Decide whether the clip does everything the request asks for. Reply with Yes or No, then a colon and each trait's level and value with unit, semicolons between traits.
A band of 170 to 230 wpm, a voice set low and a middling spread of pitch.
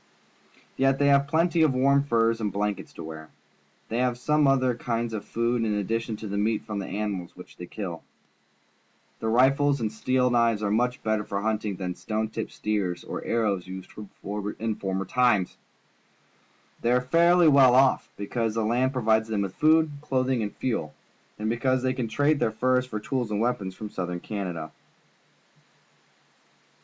Yes: average, 175 wpm; low, 115 Hz; average, 3.8 semitones